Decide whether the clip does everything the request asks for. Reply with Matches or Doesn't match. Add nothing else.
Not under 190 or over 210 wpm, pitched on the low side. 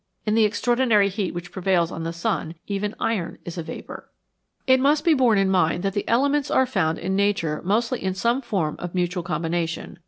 Doesn't match